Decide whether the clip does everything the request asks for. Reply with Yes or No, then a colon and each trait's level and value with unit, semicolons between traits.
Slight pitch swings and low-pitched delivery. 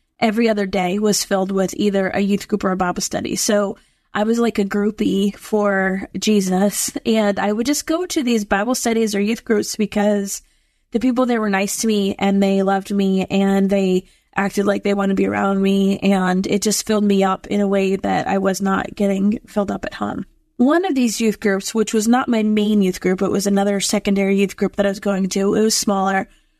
No: narrow, 1.8 semitones; high, 200 Hz